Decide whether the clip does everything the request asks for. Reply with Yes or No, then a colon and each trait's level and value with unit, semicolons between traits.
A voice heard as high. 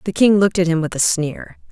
No: medium, 180 Hz